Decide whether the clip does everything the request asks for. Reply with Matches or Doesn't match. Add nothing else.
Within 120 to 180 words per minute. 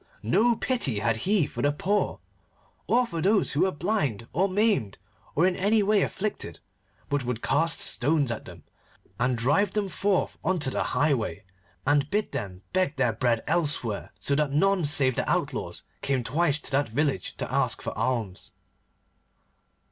Matches